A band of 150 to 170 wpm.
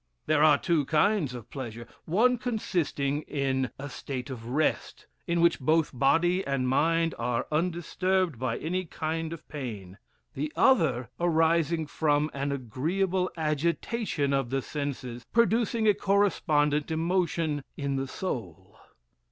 No: slow, 135 wpm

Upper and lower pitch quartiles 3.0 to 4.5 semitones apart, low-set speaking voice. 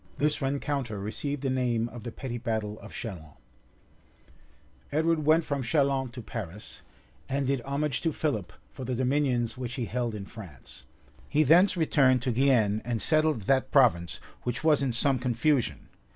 Yes: average, 3.7 semitones; low, 130 Hz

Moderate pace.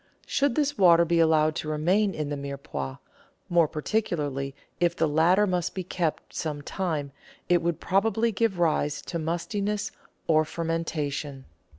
Yes: average, 150 wpm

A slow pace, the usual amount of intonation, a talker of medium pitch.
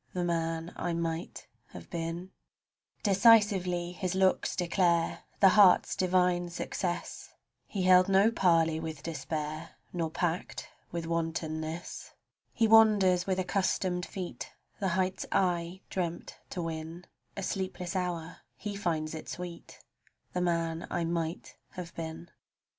No: slow, 130 wpm; narrow, 2.0 semitones; medium, 175 Hz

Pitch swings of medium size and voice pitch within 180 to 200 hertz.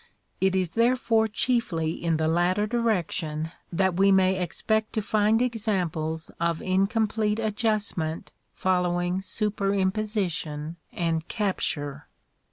Yes: average, 4.3 semitones; high, 190 Hz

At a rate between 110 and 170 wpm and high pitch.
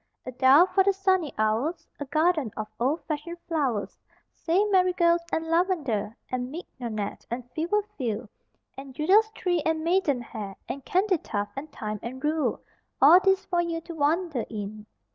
Yes: average, 155 wpm; very high, 305 Hz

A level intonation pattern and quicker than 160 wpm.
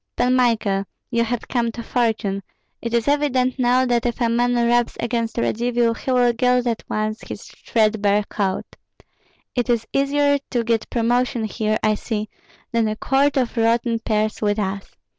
Yes: narrow, 2.2 semitones; average, 170 wpm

